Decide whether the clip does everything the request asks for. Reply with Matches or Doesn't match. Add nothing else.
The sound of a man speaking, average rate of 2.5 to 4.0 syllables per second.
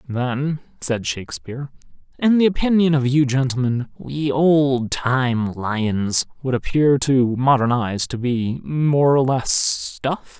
Matches